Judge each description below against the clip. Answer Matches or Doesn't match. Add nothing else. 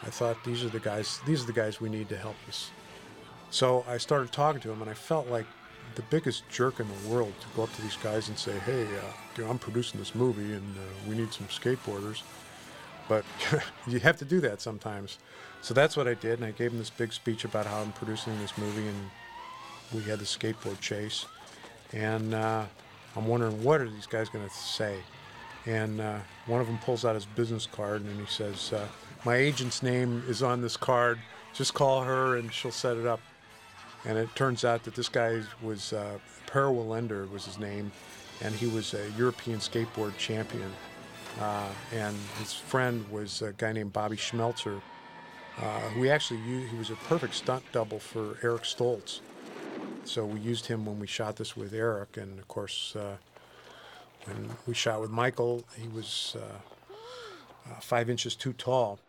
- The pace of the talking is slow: Doesn't match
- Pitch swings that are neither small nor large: Doesn't match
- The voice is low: Matches